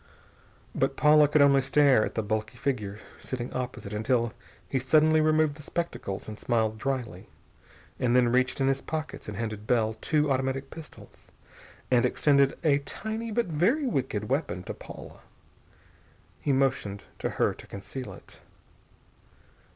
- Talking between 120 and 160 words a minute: Yes, average, 150 wpm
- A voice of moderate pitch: No, low, 130 Hz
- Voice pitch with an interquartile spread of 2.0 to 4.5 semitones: No, average, 5.0 semitones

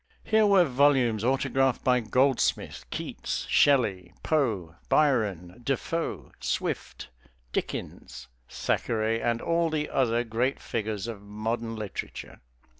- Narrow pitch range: No, average, 4.1 semitones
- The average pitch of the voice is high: No, low, 120 Hz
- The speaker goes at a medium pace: No, slow, 110 wpm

